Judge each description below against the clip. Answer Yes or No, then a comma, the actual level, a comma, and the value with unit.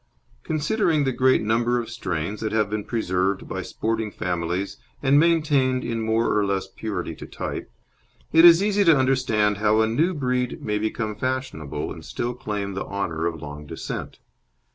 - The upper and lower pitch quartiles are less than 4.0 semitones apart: No, average, 4.7 semitones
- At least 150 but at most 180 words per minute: Yes, average, 170 wpm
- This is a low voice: Yes, low, 110 Hz